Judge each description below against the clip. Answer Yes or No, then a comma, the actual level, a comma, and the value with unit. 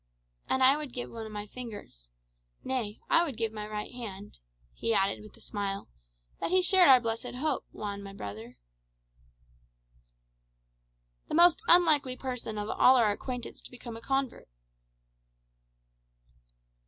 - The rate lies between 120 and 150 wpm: Yes, average, 145 wpm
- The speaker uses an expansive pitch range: No, average, 4.1 semitones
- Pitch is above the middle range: Yes, high, 230 Hz